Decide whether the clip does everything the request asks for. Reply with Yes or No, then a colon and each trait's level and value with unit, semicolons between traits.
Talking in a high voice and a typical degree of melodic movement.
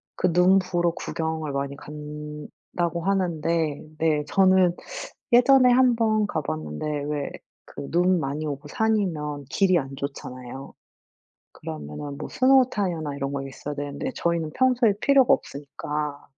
No: medium, 155 Hz; average, 4.8 semitones